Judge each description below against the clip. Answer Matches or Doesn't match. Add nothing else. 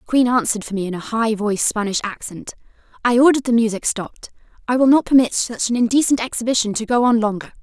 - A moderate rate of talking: Doesn't match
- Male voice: Doesn't match